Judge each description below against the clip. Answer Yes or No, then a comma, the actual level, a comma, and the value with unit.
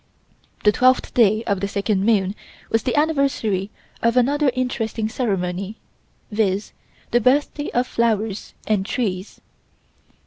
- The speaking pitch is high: Yes, high, 220 Hz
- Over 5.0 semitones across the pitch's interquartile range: No, average, 4.0 semitones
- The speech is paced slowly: Yes, slow, 130 wpm